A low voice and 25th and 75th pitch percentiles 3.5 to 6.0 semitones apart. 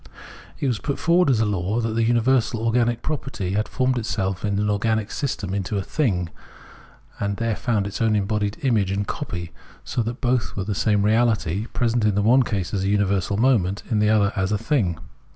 No: low, 105 Hz; average, 3.0 semitones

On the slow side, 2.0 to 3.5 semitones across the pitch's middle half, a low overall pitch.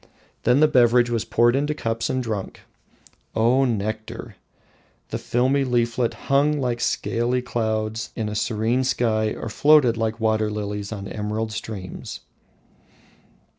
Yes: slow, 130 wpm; narrow, 2.4 semitones; low, 115 Hz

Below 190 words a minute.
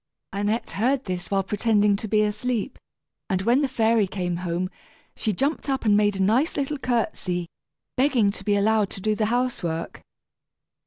Yes: average, 170 wpm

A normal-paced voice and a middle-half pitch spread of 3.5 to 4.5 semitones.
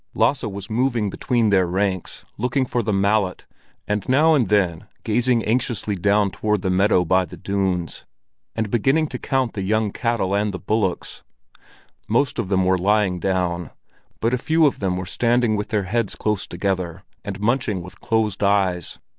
Yes: average, 175 wpm; average, 3.8 semitones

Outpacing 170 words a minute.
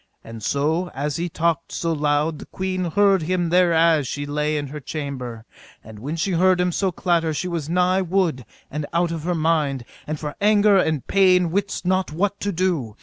Yes: average, 200 wpm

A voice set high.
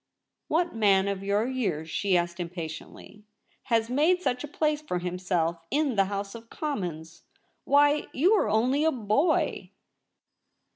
Yes: high, 215 Hz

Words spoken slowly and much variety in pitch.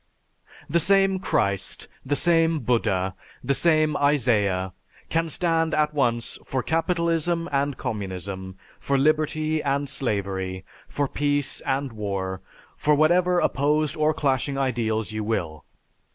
Yes: slow, 125 wpm; wide, 6.5 semitones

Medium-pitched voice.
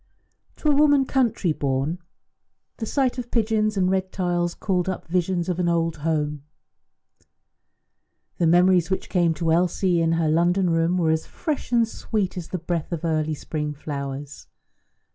Yes: medium, 175 Hz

